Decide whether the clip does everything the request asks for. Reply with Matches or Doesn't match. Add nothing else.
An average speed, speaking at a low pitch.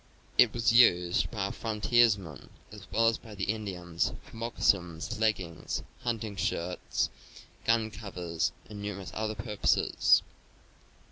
Doesn't match